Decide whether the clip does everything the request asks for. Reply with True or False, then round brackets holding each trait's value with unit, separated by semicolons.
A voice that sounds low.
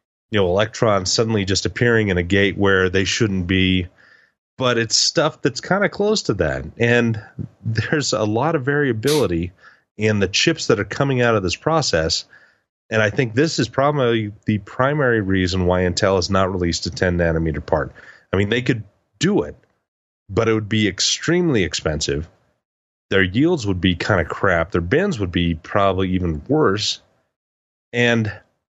True (105 Hz)